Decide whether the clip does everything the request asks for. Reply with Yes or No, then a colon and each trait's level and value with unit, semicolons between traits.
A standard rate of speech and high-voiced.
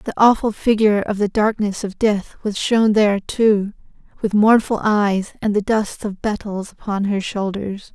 Yes: average, 175 wpm; high, 205 Hz